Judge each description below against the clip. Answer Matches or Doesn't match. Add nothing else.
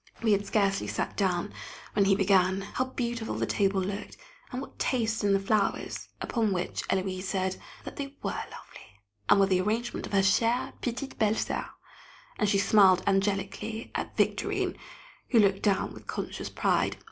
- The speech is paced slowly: Doesn't match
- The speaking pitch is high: Matches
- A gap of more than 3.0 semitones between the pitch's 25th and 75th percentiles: Doesn't match